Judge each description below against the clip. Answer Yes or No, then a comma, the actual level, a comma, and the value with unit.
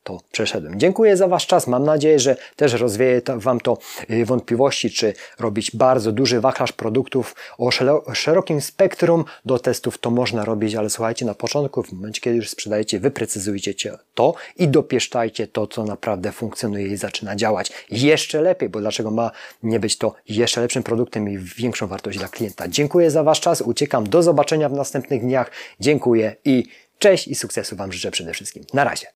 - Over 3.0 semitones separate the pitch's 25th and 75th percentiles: Yes, average, 4.2 semitones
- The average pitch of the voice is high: No, low, 120 Hz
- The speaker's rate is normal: No, fast, 175 wpm